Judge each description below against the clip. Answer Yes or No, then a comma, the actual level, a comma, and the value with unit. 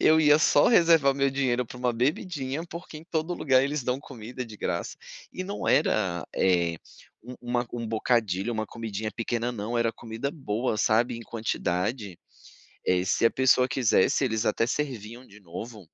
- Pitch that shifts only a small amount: No, average, 3.9 semitones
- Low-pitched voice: Yes, low, 120 Hz